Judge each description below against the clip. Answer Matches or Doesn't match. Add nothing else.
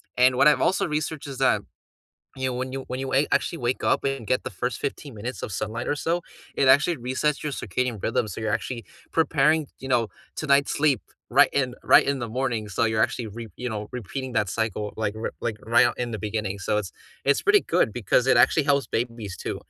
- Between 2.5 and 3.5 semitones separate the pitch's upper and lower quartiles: Doesn't match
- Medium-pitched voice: Doesn't match